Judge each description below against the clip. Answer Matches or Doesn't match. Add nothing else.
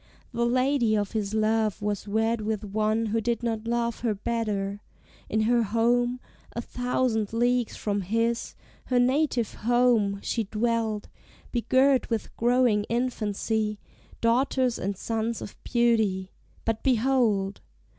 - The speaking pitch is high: Matches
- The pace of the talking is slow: Matches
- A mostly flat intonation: Matches